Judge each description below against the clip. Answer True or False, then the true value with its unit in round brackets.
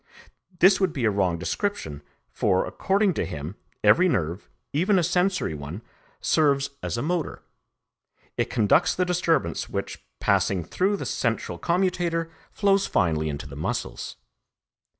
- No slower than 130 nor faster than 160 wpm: True (140 wpm)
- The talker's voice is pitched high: False (145 Hz)